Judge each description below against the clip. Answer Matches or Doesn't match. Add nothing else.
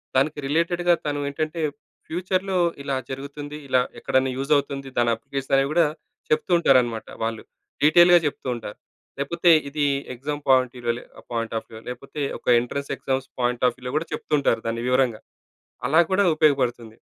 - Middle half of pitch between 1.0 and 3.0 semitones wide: Doesn't match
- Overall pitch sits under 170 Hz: Matches